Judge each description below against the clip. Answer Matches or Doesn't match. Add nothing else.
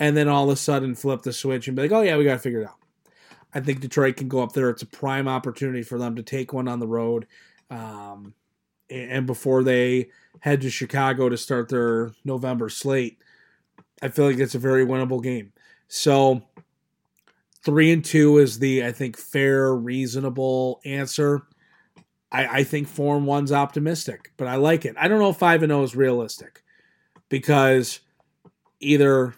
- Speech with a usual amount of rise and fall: Doesn't match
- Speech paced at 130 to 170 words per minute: Doesn't match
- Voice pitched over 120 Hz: Matches